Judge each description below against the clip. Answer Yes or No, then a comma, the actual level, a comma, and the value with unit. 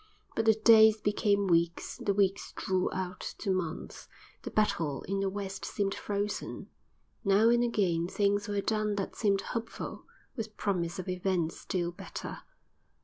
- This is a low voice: No, high, 200 Hz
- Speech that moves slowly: No, average, 150 wpm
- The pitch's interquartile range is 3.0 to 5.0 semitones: No, narrow, 2.4 semitones